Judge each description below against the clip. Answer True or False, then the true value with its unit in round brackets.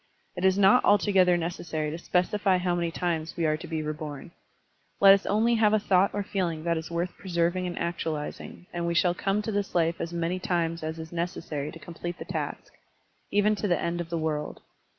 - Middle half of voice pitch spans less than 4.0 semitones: True (2.5 semitones)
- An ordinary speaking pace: False (215 wpm)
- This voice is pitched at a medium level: True (175 Hz)